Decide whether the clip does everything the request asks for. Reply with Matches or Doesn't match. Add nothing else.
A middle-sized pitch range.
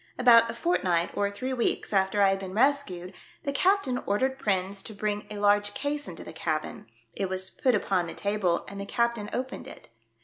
Matches